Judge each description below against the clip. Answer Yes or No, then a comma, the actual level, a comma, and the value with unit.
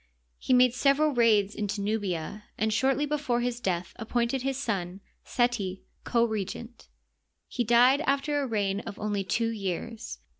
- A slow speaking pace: No, average, 150 wpm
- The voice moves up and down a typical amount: Yes, average, 3.6 semitones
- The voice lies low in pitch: No, high, 230 Hz